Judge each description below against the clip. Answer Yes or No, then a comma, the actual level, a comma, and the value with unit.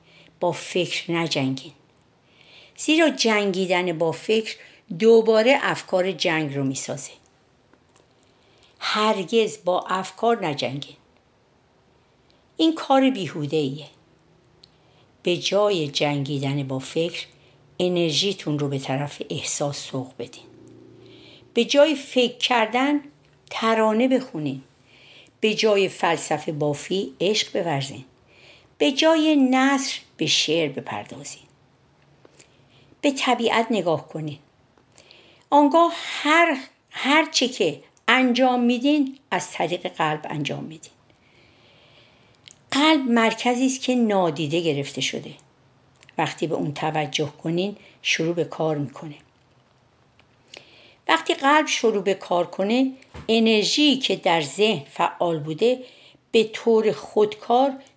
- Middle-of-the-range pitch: Yes, medium, 180 Hz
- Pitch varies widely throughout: Yes, wide, 8.3 semitones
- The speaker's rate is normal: No, slow, 100 wpm